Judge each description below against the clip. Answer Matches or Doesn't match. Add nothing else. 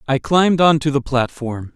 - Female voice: Doesn't match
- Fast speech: Doesn't match